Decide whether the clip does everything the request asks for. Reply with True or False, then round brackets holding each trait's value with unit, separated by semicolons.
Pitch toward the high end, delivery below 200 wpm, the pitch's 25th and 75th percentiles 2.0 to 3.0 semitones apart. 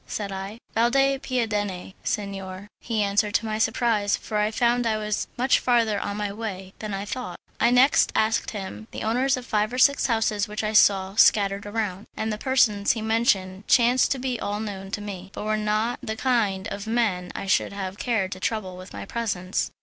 False (215 Hz; 205 wpm; 2.7 semitones)